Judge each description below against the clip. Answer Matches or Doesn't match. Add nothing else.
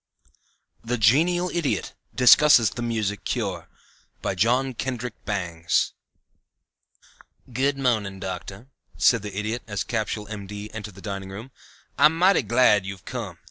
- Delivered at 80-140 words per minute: Matches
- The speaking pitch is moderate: Doesn't match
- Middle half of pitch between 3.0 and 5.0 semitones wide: Matches